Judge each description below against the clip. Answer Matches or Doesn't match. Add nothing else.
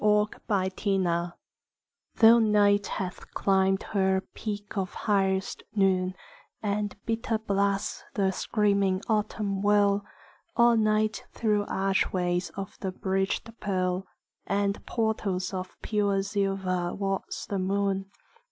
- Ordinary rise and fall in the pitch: Doesn't match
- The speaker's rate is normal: Doesn't match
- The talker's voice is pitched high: Matches